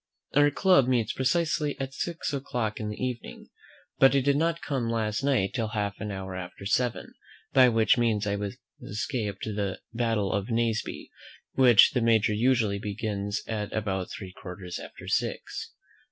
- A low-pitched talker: Yes, low, 115 Hz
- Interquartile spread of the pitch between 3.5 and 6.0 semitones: Yes, average, 4.2 semitones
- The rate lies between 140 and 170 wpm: Yes, average, 160 wpm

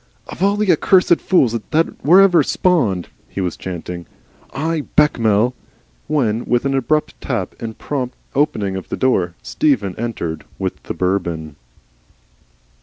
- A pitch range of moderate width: No, wide, 8.5 semitones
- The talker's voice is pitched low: Yes, low, 120 Hz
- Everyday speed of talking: Yes, average, 145 wpm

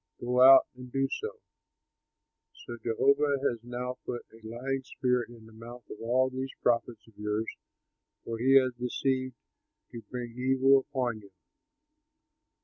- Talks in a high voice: No, low, 125 Hz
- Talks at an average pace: Yes, average, 145 wpm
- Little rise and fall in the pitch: Yes, narrow, 2.1 semitones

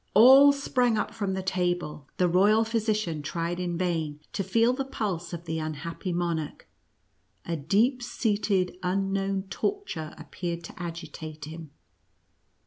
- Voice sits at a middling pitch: Yes, medium, 180 Hz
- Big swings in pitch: No, average, 4.5 semitones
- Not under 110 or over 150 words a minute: Yes, average, 145 wpm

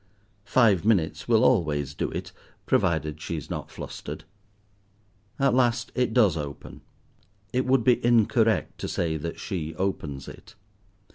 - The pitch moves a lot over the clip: Yes, wide, 7.2 semitones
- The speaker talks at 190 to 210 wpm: No, average, 140 wpm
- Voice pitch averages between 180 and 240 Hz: No, low, 100 Hz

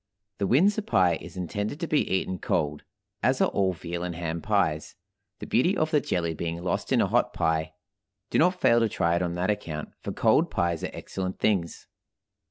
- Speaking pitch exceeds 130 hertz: No, very low, 90 Hz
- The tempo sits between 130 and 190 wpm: No, average, 200 wpm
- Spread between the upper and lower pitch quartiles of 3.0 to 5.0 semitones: No, wide, 5.4 semitones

